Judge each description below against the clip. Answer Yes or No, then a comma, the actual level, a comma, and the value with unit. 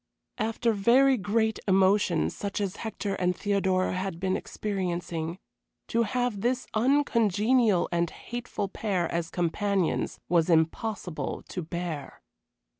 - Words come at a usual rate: No, slow, 115 wpm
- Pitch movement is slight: No, average, 3.9 semitones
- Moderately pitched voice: No, high, 195 Hz